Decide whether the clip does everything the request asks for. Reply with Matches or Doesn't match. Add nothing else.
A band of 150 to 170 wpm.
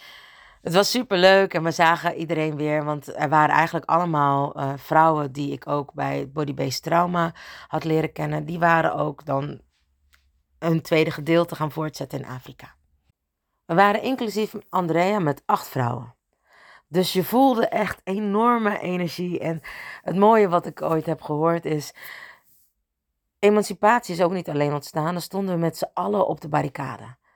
Matches